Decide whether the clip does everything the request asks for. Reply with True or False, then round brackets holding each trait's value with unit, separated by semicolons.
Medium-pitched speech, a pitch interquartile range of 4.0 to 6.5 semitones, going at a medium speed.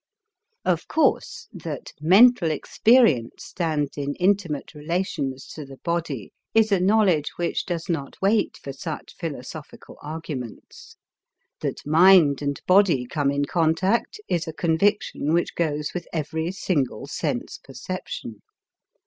False (160 Hz; 4.4 semitones; 125 wpm)